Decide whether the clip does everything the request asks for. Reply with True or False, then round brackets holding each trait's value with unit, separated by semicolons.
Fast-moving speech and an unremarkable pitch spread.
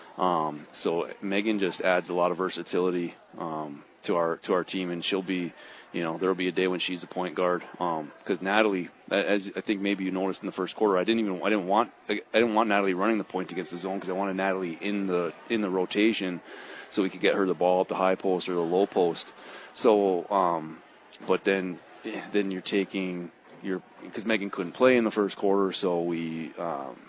False (225 wpm; 2.1 semitones)